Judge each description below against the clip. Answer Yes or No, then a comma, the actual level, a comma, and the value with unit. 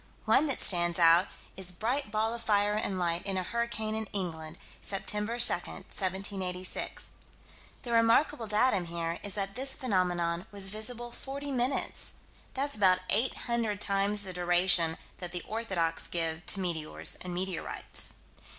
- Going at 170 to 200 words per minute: No, average, 145 wpm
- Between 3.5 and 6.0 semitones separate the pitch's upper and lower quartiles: Yes, average, 4.4 semitones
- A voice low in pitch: No, high, 195 Hz